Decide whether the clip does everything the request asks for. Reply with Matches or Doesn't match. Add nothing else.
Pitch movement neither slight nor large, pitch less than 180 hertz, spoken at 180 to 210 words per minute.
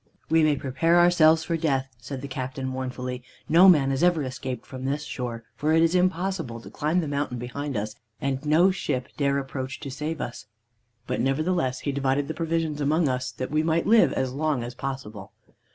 Matches